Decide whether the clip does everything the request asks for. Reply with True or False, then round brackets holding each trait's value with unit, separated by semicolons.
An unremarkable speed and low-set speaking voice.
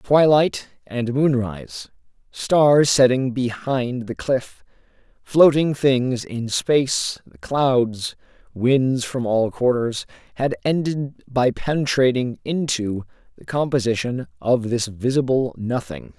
False (105 wpm; 125 Hz)